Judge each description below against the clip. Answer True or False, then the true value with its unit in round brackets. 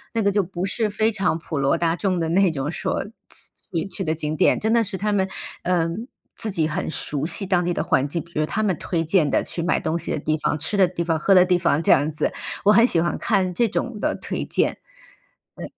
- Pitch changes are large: False (3.7 semitones)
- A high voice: False (175 Hz)